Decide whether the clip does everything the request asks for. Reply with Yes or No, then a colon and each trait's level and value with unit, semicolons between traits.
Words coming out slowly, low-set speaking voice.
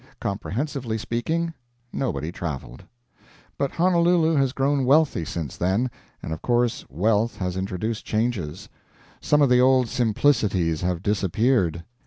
Yes: slow, 125 wpm; low, 115 Hz